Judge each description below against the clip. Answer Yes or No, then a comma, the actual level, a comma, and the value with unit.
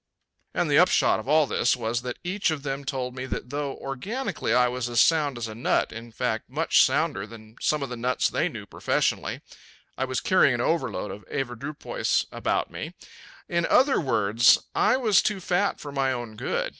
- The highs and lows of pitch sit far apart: No, average, 4.3 semitones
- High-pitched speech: No, low, 130 Hz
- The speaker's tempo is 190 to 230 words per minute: Yes, average, 200 wpm